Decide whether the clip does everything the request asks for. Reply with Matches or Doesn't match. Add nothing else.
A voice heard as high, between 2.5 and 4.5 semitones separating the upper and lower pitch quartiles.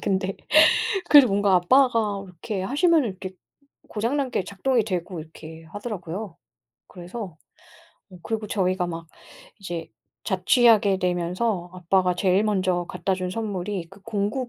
Matches